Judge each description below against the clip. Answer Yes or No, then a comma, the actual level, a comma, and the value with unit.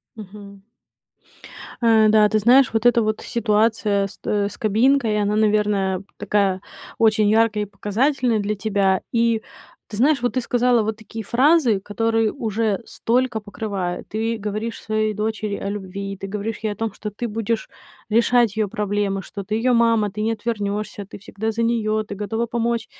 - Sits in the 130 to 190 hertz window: No, high, 215 Hz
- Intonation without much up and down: Yes, narrow, 1.9 semitones